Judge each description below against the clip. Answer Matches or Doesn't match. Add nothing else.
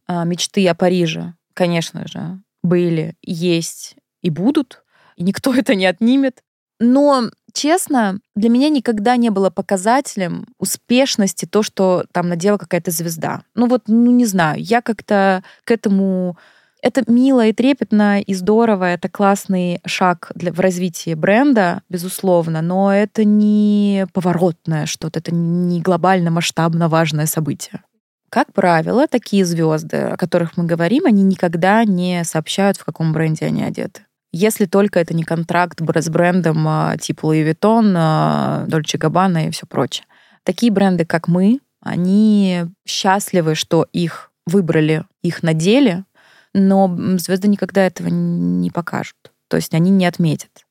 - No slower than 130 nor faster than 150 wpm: Matches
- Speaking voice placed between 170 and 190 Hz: Matches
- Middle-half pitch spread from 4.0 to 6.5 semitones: Doesn't match